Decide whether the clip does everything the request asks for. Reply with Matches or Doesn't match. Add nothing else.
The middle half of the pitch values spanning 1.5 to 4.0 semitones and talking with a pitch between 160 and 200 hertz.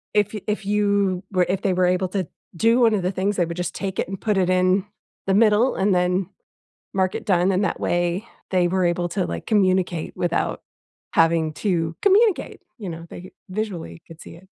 Matches